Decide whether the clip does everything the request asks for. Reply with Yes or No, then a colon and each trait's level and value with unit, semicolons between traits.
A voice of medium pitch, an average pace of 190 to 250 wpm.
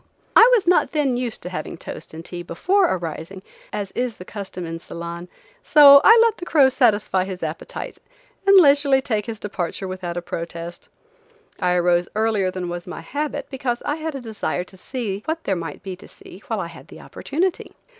No: high, 200 Hz; average, 195 wpm